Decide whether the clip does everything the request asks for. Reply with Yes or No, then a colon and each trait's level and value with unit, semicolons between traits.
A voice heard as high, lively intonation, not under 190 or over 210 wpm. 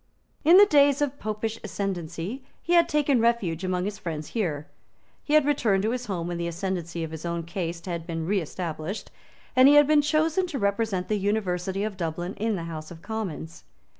Yes: high, 195 Hz; wide, 6.6 semitones; average, 195 wpm